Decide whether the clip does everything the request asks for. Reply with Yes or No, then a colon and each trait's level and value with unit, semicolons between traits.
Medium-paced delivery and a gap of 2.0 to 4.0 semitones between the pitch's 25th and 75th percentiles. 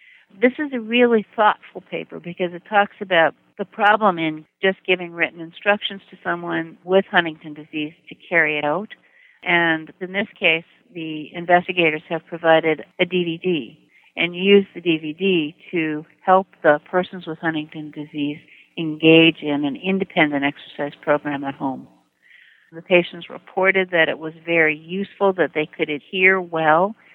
Yes: average, 150 wpm; average, 3.5 semitones